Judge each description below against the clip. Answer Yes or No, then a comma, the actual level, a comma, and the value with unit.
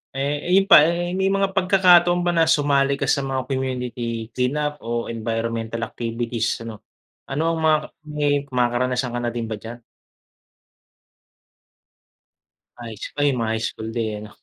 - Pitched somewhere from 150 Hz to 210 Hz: No, low, 130 Hz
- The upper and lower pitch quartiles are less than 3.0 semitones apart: No, average, 4.4 semitones